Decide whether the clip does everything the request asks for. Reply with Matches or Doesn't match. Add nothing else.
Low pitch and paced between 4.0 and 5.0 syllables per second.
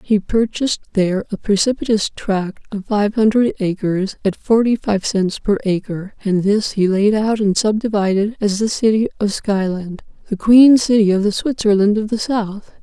Doesn't match